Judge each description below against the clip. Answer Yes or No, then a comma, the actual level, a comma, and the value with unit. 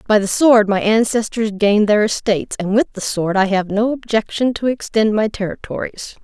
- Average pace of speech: Yes, average, 190 wpm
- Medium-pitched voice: No, high, 215 Hz